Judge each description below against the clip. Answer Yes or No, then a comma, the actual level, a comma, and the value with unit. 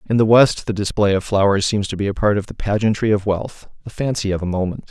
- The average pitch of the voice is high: No, low, 105 Hz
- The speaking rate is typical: No, fast, 255 wpm